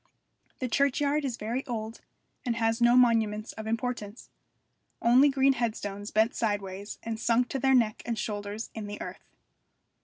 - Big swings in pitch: No, average, 2.7 semitones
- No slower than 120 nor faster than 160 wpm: Yes, average, 155 wpm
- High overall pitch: Yes, high, 230 Hz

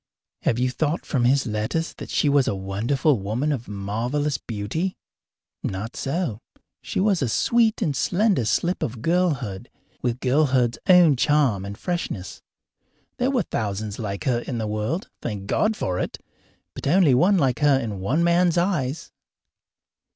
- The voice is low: Yes, low, 130 Hz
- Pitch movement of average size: No, wide, 7.3 semitones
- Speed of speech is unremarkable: Yes, average, 160 wpm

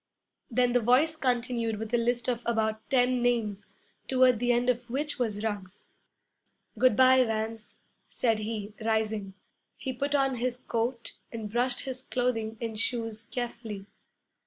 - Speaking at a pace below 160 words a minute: Yes, average, 150 wpm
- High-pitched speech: Yes, high, 235 Hz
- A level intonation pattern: Yes, narrow, 2.3 semitones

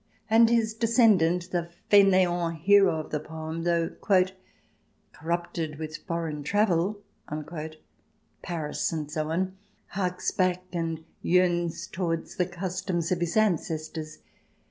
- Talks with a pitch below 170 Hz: No, medium, 175 Hz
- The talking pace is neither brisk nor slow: No, slow, 120 wpm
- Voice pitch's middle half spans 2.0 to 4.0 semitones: Yes, narrow, 2.5 semitones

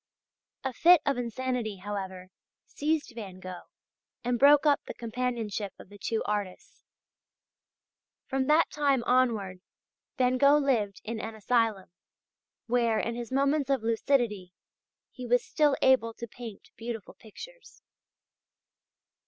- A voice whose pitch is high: Yes, high, 235 Hz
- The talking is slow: Yes, slow, 130 wpm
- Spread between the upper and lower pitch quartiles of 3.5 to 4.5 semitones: Yes, average, 4.1 semitones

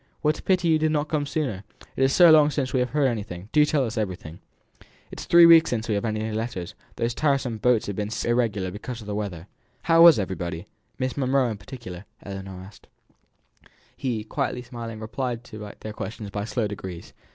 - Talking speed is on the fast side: Yes, fast, 210 wpm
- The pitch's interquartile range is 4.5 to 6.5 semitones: Yes, average, 5.0 semitones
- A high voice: No, low, 115 Hz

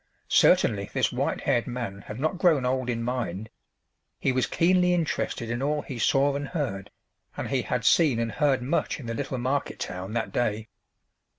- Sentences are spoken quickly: No, average, 185 wpm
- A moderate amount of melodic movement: Yes, average, 3.8 semitones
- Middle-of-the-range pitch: No, low, 125 Hz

